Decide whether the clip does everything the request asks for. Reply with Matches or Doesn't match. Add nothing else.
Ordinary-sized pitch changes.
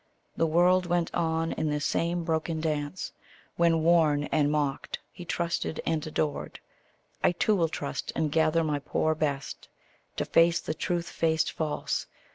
Doesn't match